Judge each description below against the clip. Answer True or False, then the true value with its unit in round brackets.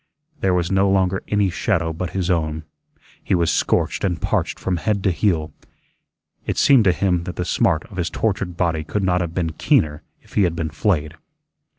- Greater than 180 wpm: True (200 wpm)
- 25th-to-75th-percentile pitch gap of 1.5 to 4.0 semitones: True (2.9 semitones)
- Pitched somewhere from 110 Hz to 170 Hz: False (90 Hz)